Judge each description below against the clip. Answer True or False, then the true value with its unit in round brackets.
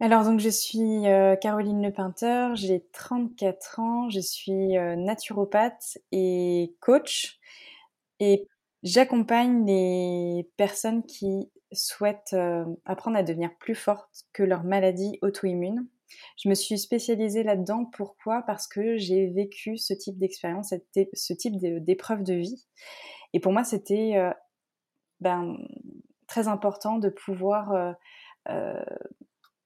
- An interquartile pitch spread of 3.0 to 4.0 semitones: True (3.3 semitones)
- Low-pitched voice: False (205 Hz)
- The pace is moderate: False (115 wpm)